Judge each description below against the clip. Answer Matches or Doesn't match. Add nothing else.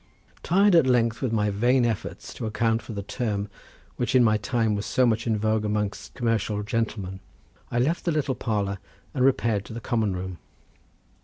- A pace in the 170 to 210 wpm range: Matches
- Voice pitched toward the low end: Matches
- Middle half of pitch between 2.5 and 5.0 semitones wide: Matches